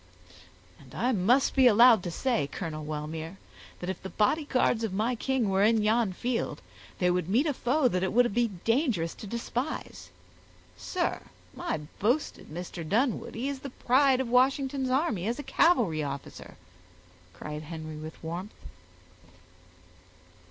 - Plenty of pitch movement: Yes, wide, 6.5 semitones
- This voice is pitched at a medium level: No, high, 225 Hz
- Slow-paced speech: No, average, 150 wpm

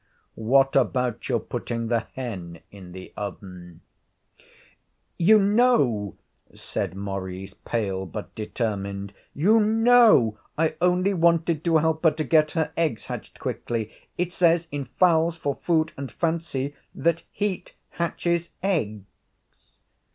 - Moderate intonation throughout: No, wide, 8.0 semitones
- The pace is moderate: No, slow, 125 wpm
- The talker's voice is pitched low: No, medium, 145 Hz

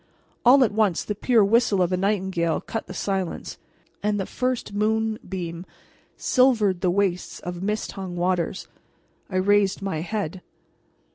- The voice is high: Yes, high, 195 Hz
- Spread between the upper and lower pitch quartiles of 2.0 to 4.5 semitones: Yes, average, 2.9 semitones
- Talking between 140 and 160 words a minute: Yes, average, 145 wpm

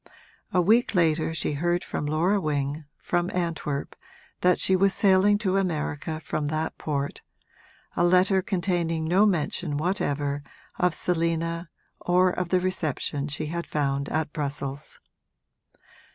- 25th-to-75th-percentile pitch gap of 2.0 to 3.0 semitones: No, average, 3.4 semitones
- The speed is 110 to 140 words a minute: Yes, slow, 135 wpm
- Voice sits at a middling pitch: Yes, medium, 165 Hz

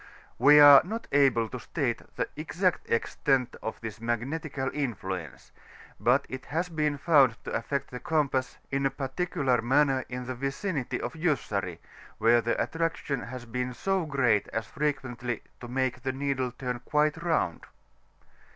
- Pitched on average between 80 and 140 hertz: Yes, low, 135 Hz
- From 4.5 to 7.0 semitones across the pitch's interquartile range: No, average, 3.5 semitones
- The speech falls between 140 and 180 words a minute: Yes, average, 150 wpm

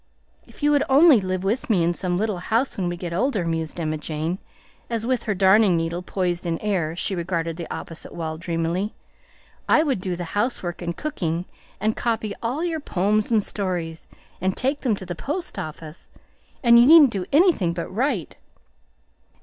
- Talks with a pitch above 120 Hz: Yes, high, 190 Hz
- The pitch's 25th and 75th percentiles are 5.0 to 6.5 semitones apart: Yes, wide, 5.5 semitones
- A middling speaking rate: Yes, average, 185 wpm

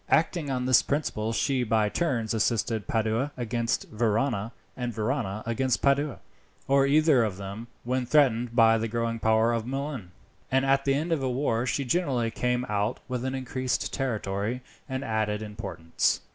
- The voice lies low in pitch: Yes, low, 120 Hz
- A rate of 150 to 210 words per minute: Yes, average, 165 wpm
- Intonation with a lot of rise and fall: No, average, 3.3 semitones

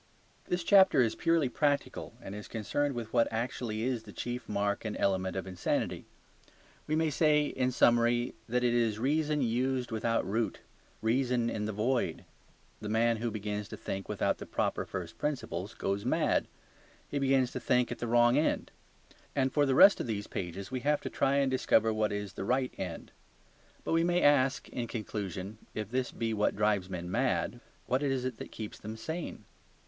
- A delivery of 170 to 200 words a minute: Yes, average, 190 wpm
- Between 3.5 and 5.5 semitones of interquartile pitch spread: Yes, average, 4.0 semitones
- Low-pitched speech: Yes, low, 120 Hz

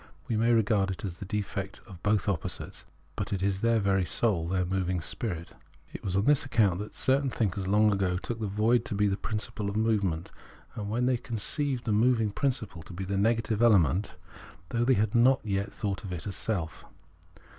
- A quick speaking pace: Yes, fast, 210 wpm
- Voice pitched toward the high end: No, low, 105 Hz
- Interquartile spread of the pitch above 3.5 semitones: No, average, 3.0 semitones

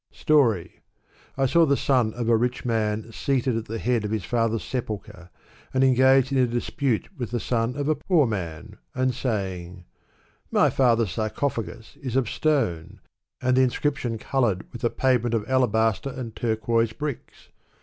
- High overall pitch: No, low, 120 Hz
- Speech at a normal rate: Yes, average, 170 wpm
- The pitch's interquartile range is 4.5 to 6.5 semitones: No, average, 3.3 semitones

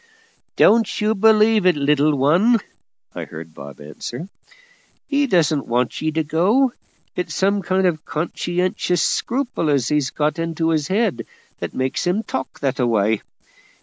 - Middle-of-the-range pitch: Yes, medium, 165 Hz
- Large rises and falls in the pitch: Yes, wide, 6.3 semitones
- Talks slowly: No, average, 150 wpm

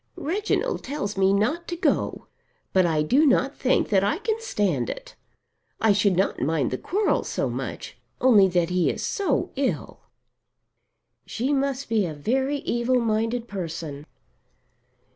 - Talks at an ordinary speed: Yes, average, 150 wpm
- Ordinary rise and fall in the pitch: No, wide, 7.3 semitones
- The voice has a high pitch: Yes, high, 225 Hz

